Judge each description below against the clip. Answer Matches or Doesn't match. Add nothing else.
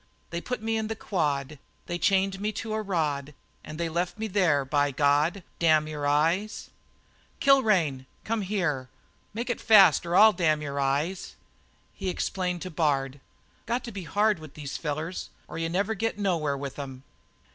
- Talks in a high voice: Doesn't match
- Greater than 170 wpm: Matches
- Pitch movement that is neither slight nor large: Doesn't match